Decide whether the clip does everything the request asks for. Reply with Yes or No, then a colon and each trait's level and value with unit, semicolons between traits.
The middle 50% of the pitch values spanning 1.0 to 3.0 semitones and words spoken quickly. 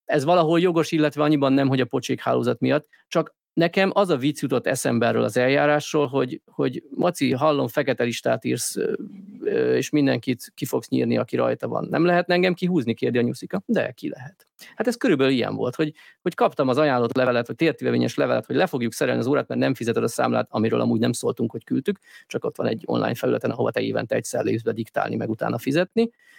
No: wide, 5.6 semitones; fast, 215 wpm